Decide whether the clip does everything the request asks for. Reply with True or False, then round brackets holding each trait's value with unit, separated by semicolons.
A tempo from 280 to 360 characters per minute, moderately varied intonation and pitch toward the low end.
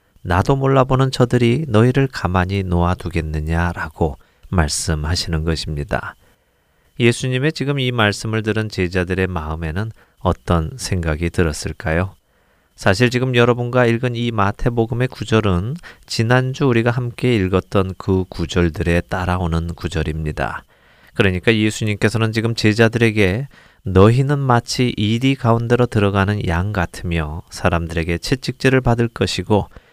False (315 characters per minute; 5.7 semitones; 100 Hz)